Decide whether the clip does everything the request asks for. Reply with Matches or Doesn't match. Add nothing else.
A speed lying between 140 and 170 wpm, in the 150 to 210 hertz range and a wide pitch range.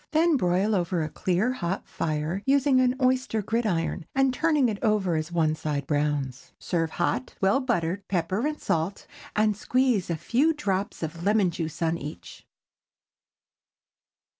Matches